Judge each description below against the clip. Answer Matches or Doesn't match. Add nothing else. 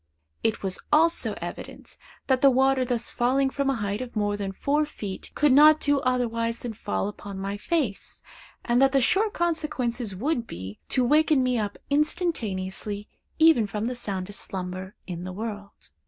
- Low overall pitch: Doesn't match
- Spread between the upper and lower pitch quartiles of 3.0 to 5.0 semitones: Doesn't match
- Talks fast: Doesn't match